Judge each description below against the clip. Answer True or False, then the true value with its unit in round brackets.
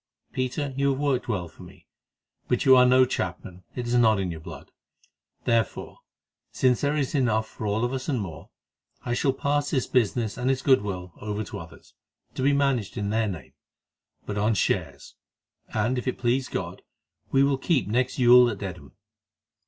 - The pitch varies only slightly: False (4.1 semitones)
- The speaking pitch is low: True (120 Hz)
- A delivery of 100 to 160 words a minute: False (185 wpm)